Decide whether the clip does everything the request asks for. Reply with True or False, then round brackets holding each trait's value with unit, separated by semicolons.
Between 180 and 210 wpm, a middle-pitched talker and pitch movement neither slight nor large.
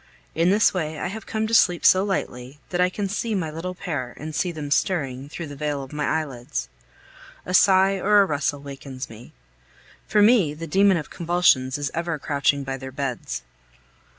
True (195 wpm; 155 Hz; 4.9 semitones)